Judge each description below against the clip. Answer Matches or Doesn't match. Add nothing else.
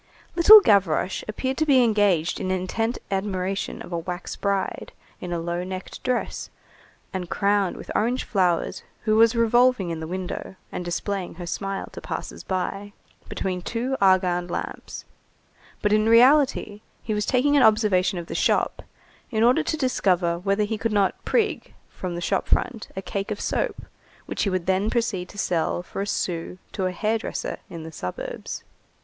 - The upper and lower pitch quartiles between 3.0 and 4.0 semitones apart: Matches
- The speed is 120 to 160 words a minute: Doesn't match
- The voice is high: Matches